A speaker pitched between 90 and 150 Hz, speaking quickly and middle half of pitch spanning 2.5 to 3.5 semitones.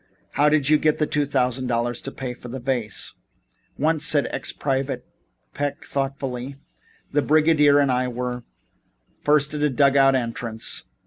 No: low, 135 Hz; average, 165 wpm; average, 2.8 semitones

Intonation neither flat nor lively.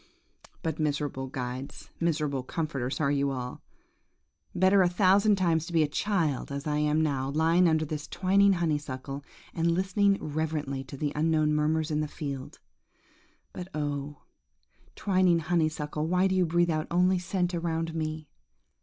Yes: average, 3.1 semitones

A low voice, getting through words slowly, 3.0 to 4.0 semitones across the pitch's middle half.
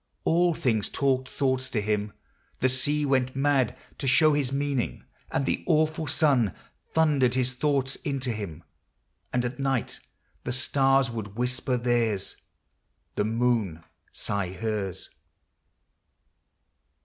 Yes: low, 130 Hz; slow, 125 wpm; average, 3.6 semitones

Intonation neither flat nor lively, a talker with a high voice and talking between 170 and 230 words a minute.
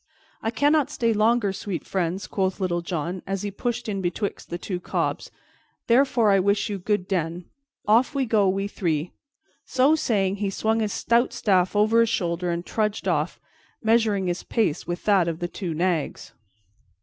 Yes: average, 3.8 semitones; high, 200 Hz; average, 175 wpm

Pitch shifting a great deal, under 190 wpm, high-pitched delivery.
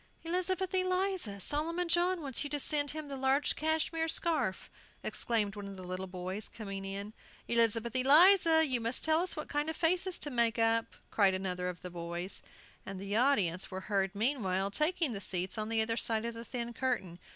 No: wide, 8.1 semitones; average, 195 wpm; high, 235 Hz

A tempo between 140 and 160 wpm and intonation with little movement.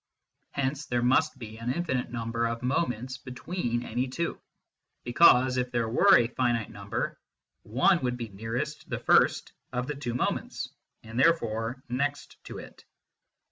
Yes: average, 150 wpm; narrow, 2.1 semitones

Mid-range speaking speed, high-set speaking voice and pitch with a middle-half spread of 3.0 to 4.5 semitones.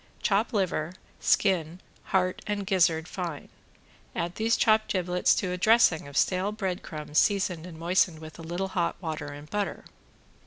No: average, 160 wpm; medium, 180 Hz; average, 3.4 semitones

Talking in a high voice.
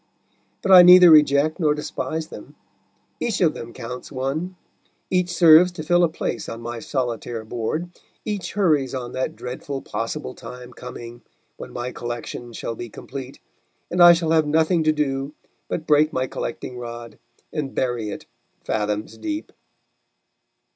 No: medium, 140 Hz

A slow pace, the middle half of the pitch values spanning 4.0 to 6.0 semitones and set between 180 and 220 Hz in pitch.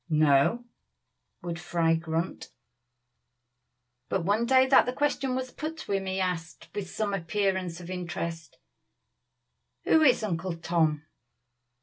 Yes: slow, 125 wpm; wide, 5.6 semitones; medium, 185 Hz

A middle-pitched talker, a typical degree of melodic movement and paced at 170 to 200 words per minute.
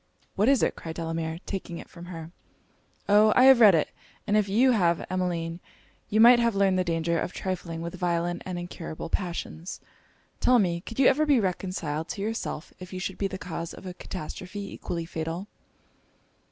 Yes: medium, 180 Hz; average, 3.4 semitones; average, 190 wpm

